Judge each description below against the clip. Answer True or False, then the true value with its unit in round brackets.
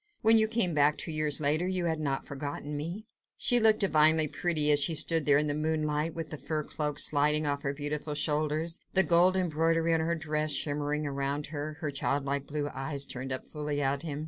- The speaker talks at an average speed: False (210 wpm)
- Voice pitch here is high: False (150 Hz)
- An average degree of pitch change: False (2.1 semitones)